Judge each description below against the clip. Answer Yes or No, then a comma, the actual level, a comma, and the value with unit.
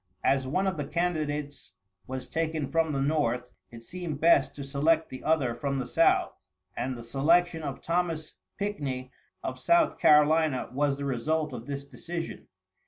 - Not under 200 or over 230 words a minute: No, average, 165 wpm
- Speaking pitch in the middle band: Yes, medium, 150 Hz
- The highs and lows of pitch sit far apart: No, average, 3.2 semitones